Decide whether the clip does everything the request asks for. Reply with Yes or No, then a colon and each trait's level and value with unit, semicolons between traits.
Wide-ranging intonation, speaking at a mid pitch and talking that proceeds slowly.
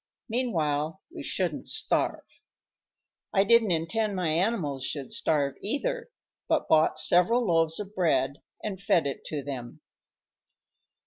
Yes: wide, 6.1 semitones; medium, 170 Hz; slow, 125 wpm